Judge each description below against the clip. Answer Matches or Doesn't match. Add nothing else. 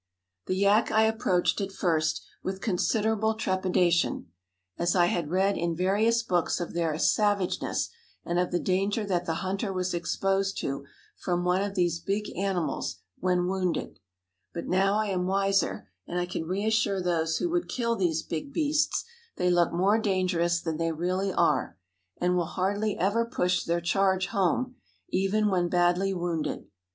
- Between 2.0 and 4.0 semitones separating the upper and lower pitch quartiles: Matches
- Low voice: Doesn't match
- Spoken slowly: Doesn't match